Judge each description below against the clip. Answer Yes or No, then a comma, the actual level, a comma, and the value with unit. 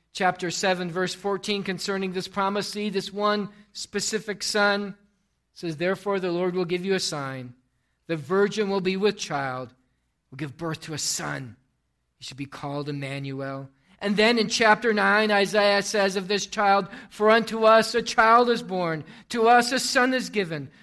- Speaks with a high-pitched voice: Yes, high, 195 Hz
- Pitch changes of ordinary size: Yes, average, 4.5 semitones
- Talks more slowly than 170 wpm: No, average, 175 wpm